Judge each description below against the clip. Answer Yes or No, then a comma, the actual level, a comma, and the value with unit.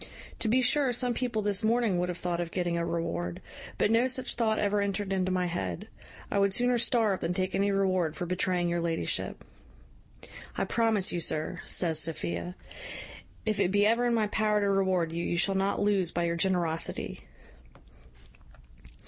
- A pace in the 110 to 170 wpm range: No, average, 180 wpm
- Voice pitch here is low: No, high, 190 Hz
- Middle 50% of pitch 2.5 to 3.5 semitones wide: No, average, 3.9 semitones